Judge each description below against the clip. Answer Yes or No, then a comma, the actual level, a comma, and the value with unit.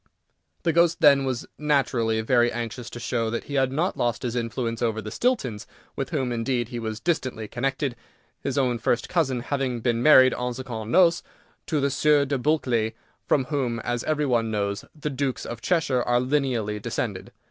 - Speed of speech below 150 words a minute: No, average, 185 wpm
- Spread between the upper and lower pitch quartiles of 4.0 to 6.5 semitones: No, average, 3.3 semitones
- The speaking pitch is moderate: No, low, 125 Hz